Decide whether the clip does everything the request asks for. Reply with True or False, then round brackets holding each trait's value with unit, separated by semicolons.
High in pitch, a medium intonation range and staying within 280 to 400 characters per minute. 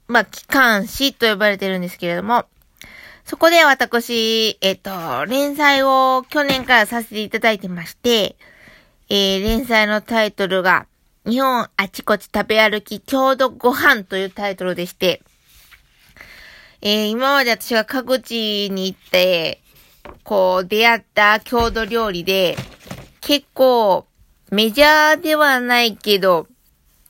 False (220 Hz; 4.7 semitones; 250 characters per minute)